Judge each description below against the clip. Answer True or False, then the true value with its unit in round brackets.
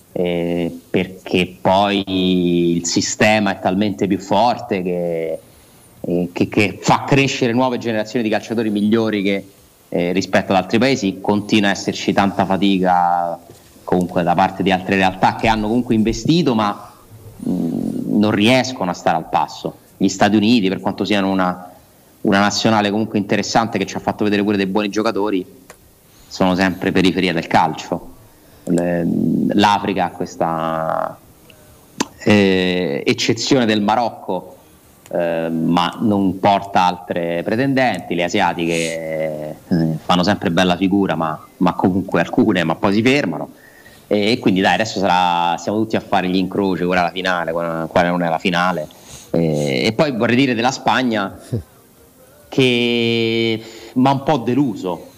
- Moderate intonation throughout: True (3.5 semitones)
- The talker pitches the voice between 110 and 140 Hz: False (95 Hz)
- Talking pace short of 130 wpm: False (145 wpm)